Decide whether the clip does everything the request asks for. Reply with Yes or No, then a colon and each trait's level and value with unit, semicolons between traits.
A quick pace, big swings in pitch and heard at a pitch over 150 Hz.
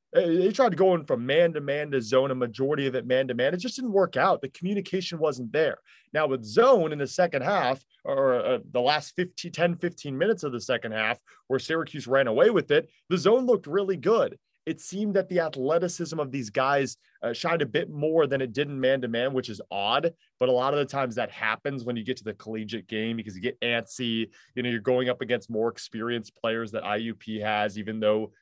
No: fast, 240 wpm; wide, 6.6 semitones; low, 135 Hz